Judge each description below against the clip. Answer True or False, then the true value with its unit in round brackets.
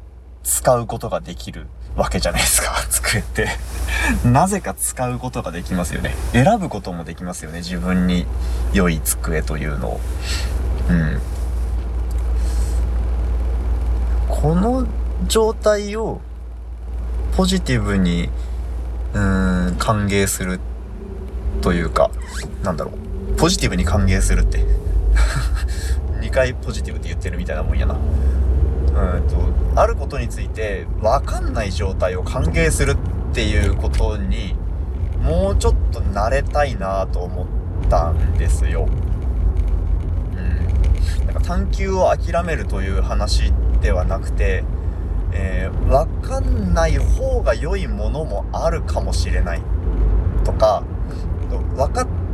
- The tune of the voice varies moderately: True (4.3 semitones)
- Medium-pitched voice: False (85 Hz)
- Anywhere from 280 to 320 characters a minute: False (240 characters per minute)